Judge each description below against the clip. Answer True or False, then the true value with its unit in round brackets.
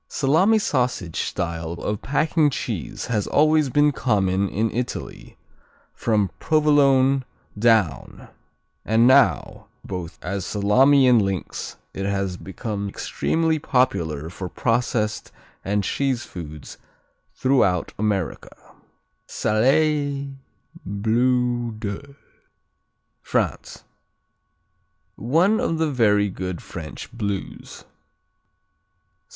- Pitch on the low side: True (115 Hz)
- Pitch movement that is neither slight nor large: False (5.9 semitones)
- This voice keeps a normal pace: False (90 wpm)